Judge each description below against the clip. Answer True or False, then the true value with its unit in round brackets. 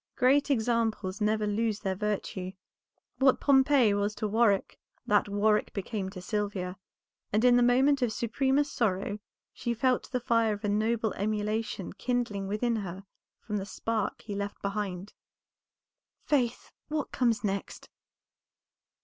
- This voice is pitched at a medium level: False (215 Hz)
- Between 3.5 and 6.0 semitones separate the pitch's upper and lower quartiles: False (3.1 semitones)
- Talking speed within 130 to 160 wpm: True (140 wpm)